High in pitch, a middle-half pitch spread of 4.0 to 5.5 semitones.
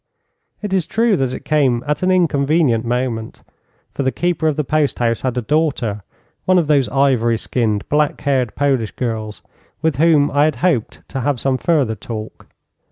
No: low, 135 Hz; average, 4.6 semitones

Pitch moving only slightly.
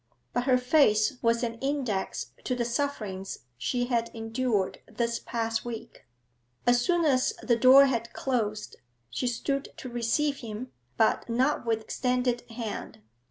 Yes: narrow, 2.2 semitones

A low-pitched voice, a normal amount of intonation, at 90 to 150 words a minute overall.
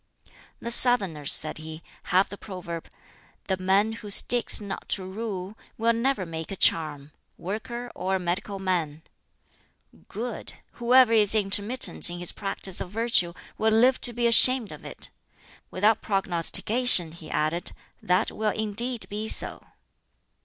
No: high, 200 Hz; average, 4.3 semitones; average, 145 wpm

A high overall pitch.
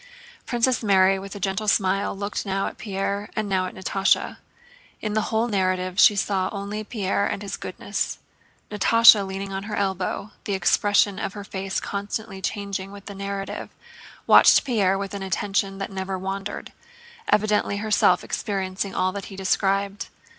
Yes: high, 200 Hz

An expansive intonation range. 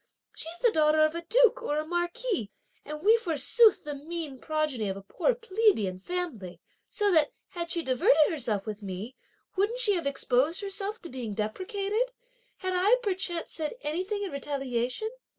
Yes: wide, 7.0 semitones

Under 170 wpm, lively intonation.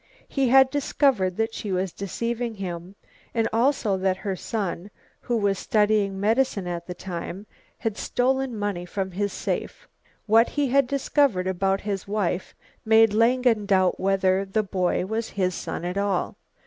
No: average, 160 wpm; average, 3.4 semitones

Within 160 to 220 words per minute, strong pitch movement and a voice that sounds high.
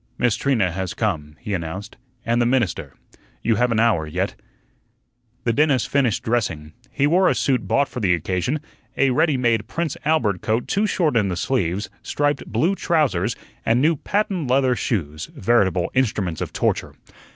No: average, 170 wpm; wide, 6.7 semitones; low, 115 Hz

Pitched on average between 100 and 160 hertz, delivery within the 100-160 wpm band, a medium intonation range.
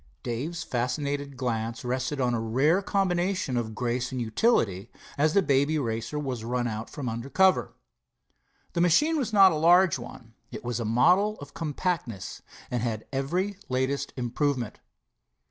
No: low, 135 Hz; average, 155 wpm; wide, 6.1 semitones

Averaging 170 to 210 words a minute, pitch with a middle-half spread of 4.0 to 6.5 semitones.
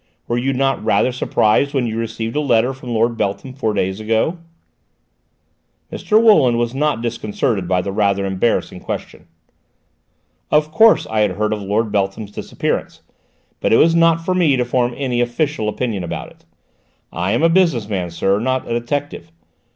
Yes: average, 175 wpm; average, 4.6 semitones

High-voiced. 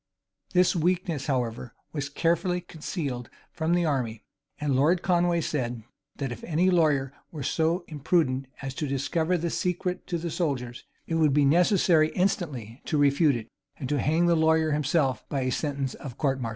No: medium, 150 Hz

